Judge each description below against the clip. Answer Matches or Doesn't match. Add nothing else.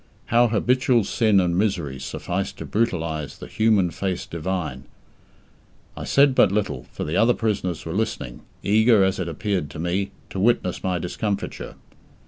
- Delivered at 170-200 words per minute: Doesn't match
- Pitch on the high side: Doesn't match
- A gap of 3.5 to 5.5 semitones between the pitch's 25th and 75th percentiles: Matches